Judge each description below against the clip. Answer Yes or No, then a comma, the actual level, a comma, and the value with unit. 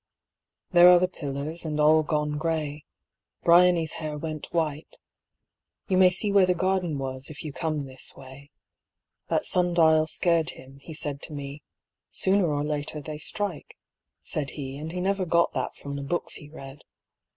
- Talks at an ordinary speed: Yes, average, 175 wpm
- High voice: No, medium, 155 Hz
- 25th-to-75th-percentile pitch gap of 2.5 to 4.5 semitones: Yes, average, 3.1 semitones